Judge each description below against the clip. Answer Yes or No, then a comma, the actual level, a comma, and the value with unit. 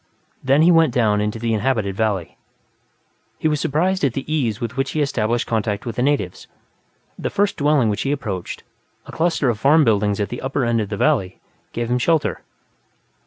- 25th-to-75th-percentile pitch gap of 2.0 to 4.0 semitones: No, average, 5.3 semitones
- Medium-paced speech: Yes, average, 195 wpm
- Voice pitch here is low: Yes, low, 120 Hz